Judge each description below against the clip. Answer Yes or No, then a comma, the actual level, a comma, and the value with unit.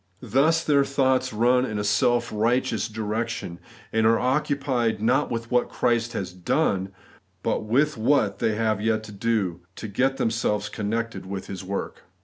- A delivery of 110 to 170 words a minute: Yes, average, 160 wpm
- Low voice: Yes, low, 115 Hz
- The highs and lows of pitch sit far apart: No, average, 3.2 semitones